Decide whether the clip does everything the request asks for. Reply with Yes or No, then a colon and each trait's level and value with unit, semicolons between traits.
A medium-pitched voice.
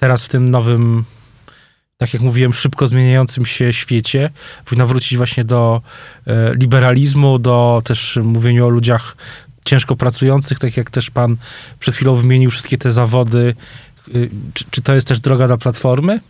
No: low, 125 Hz